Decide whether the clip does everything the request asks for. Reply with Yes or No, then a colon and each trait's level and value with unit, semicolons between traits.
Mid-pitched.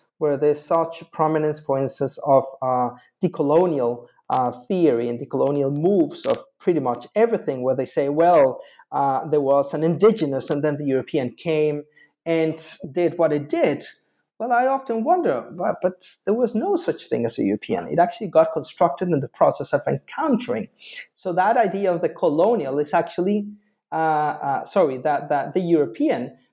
Yes: medium, 160 Hz